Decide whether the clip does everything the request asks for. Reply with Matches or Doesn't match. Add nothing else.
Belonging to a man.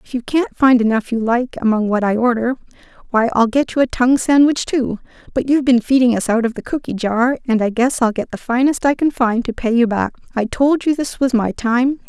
Doesn't match